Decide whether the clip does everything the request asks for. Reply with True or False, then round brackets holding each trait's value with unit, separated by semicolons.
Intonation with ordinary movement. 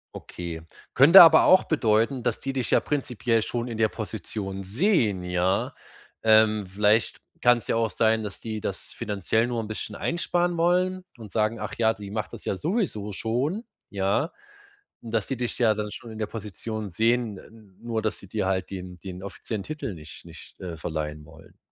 True (3.7 semitones)